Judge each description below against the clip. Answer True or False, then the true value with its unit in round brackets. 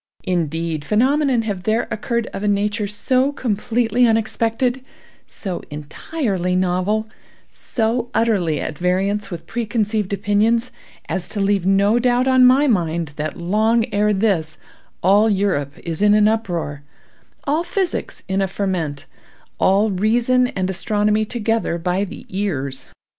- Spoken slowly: True (125 wpm)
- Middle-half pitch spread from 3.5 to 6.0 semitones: True (4.0 semitones)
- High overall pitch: True (205 Hz)